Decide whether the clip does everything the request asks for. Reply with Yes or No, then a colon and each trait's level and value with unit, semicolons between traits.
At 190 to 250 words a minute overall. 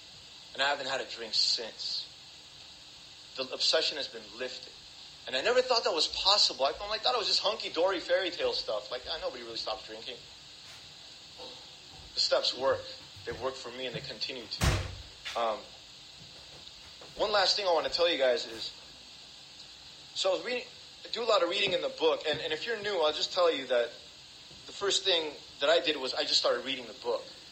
Yes: average, 200 wpm